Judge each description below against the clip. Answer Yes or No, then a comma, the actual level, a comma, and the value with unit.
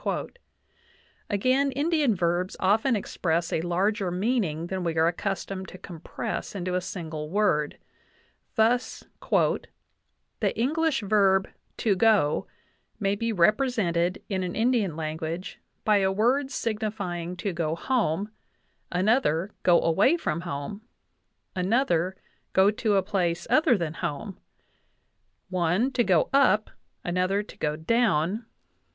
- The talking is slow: Yes, slow, 120 wpm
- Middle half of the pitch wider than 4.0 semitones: Yes, average, 4.4 semitones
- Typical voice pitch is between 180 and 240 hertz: Yes, high, 190 Hz